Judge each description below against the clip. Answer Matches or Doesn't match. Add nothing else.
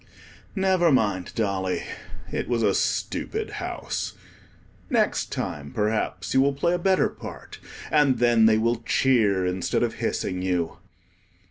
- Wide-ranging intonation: Matches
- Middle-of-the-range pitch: Doesn't match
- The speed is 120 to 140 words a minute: Matches